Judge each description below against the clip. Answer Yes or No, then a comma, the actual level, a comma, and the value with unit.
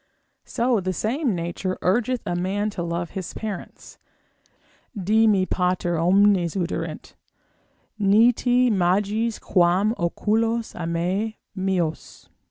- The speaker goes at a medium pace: No, slow, 110 wpm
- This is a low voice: No, high, 195 Hz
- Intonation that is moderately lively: Yes, average, 3.9 semitones